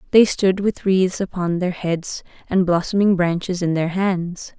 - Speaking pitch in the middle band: Yes, medium, 180 Hz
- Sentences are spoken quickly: No, average, 170 wpm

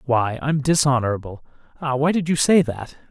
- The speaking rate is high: No, average, 175 wpm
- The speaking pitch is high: No, low, 135 Hz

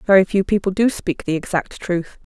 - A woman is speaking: Yes, female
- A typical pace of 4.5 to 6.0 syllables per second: Yes, 5.3 syllables/s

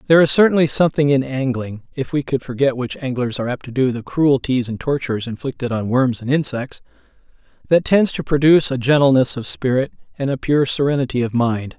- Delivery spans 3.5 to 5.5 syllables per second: No, 6.0 syllables/s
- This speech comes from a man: Yes, male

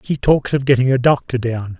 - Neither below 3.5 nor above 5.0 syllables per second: No, 5.3 syllables/s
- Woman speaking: No, male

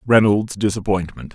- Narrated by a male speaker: Yes, male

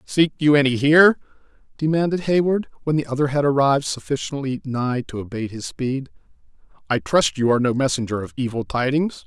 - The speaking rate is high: No, average, 170 wpm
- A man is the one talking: Yes, male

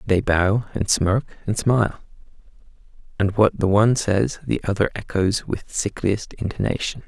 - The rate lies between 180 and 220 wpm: No, average, 145 wpm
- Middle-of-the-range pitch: No, low, 100 Hz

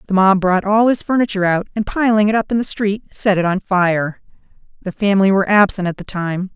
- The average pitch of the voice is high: Yes, high, 200 Hz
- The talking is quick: Yes, fast, 230 wpm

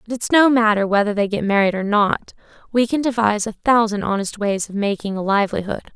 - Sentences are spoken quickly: Yes, fast, 210 wpm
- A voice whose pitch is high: Yes, high, 215 Hz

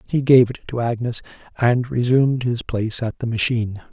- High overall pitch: No, low, 120 Hz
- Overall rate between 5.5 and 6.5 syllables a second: Yes, 5.6 syllables/s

